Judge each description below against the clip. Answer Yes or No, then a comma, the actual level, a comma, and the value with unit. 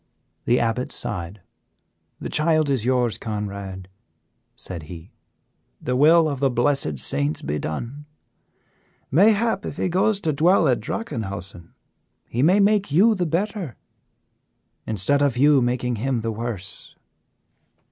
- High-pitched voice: No, low, 125 Hz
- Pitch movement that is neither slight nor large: No, wide, 7.4 semitones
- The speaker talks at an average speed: No, slow, 130 wpm